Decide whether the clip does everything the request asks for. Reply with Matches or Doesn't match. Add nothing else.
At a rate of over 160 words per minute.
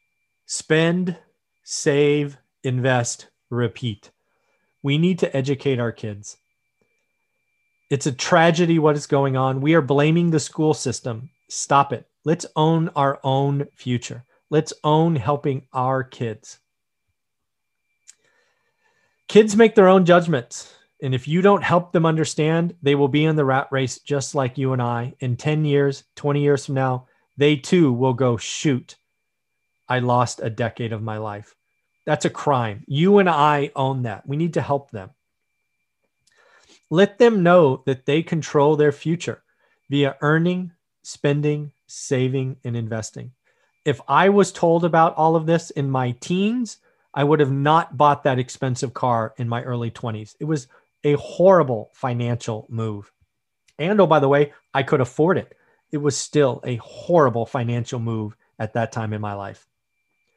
Doesn't match